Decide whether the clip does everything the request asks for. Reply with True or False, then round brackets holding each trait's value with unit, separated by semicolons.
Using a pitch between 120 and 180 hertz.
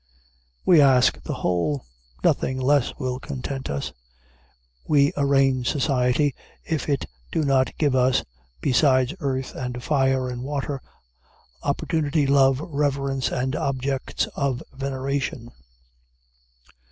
True (135 Hz)